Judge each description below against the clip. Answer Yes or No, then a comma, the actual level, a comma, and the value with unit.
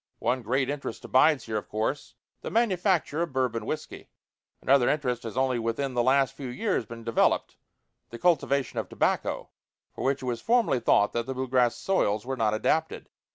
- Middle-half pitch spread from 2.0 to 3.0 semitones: No, average, 3.6 semitones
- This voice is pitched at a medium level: No, low, 130 Hz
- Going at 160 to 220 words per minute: Yes, average, 185 wpm